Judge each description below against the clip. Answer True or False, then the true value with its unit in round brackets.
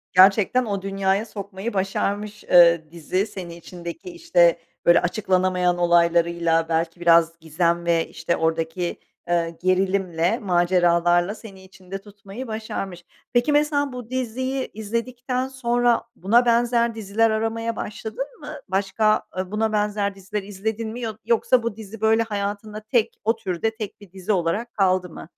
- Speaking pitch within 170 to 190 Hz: False (200 Hz)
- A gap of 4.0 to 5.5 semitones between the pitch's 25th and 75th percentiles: True (4.3 semitones)